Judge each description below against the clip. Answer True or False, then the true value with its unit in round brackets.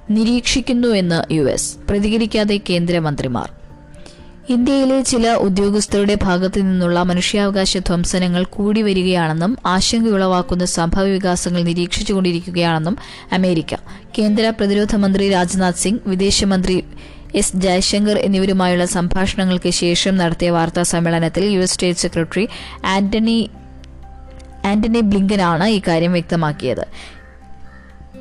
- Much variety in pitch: False (2.9 semitones)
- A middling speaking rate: True (85 wpm)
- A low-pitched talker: False (185 Hz)